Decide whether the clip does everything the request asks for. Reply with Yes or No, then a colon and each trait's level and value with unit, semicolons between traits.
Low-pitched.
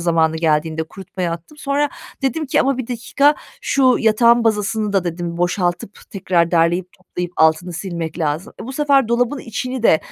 No: high, 190 Hz